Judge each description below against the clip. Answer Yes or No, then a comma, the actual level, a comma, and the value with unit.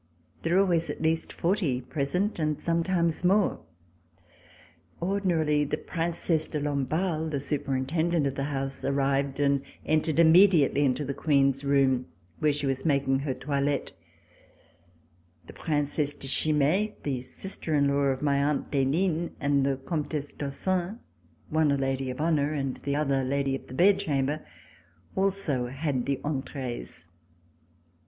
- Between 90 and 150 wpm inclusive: Yes, average, 145 wpm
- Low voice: No, medium, 145 Hz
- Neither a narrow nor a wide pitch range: Yes, average, 3.0 semitones